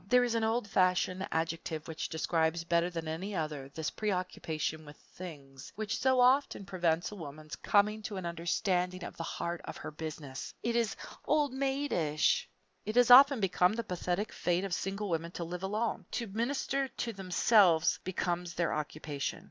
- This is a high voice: No, medium, 180 Hz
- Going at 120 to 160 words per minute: No, average, 170 wpm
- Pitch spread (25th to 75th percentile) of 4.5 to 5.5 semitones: Yes, average, 5.0 semitones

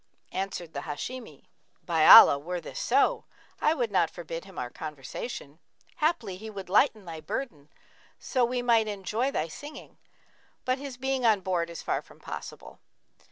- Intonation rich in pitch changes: Yes, wide, 7.0 semitones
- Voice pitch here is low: No, high, 195 Hz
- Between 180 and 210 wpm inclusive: No, average, 160 wpm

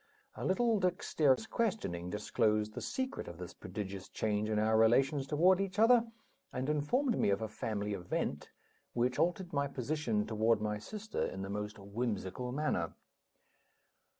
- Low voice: Yes, low, 120 Hz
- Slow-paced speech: No, average, 150 wpm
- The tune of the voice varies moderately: No, wide, 9.0 semitones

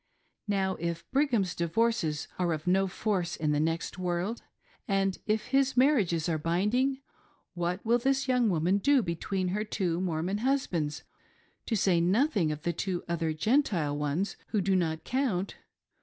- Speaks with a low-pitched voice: No, medium, 185 Hz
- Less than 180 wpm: Yes, average, 160 wpm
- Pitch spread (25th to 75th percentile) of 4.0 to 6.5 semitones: Yes, average, 5.2 semitones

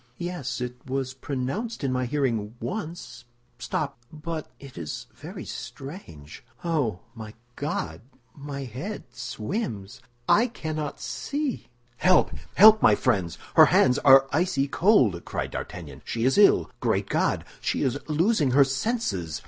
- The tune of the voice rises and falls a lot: Yes, wide, 5.9 semitones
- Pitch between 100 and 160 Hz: Yes, low, 135 Hz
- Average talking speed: No, slow, 125 wpm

